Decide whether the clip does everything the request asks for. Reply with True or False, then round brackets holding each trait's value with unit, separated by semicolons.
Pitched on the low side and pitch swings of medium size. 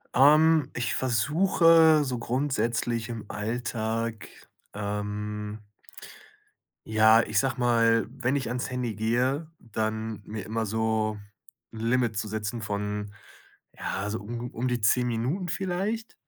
True (115 Hz; 3.0 semitones)